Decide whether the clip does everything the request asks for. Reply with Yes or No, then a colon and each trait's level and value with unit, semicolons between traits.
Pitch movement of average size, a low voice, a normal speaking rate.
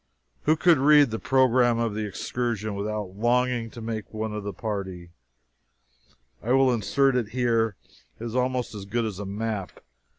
Yes: average, 3.0 semitones; low, 115 Hz; average, 170 wpm